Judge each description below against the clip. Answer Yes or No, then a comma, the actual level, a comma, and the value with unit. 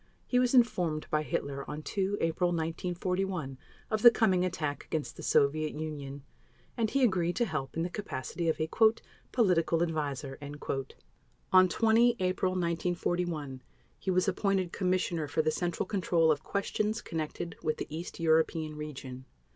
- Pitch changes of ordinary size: Yes, average, 3.5 semitones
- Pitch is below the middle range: No, medium, 170 Hz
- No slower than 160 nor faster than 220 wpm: No, average, 150 wpm